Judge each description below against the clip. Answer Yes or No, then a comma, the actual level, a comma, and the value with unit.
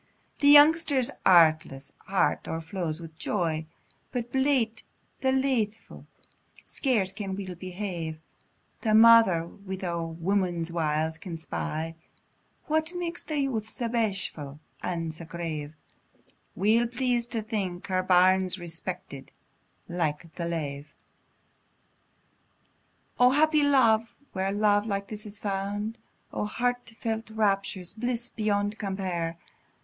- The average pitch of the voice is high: Yes, high, 195 Hz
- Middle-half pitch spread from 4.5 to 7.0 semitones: Yes, average, 5.2 semitones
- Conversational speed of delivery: No, slow, 115 wpm